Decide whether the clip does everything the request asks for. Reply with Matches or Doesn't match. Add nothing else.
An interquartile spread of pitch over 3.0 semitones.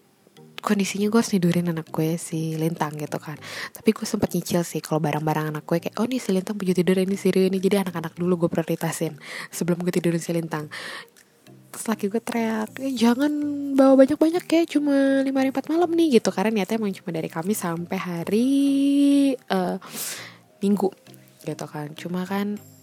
Matches